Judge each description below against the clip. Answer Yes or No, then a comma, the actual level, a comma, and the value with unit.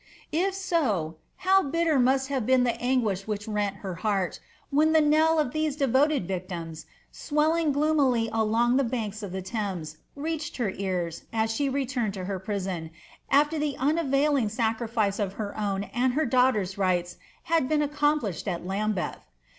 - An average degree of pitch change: No, wide, 6.8 semitones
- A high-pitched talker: Yes, high, 240 Hz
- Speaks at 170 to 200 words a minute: No, average, 160 wpm